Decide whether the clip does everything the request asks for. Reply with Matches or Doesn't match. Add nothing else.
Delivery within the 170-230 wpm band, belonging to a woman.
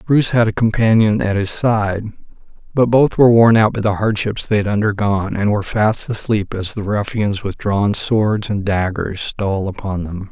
Doesn't match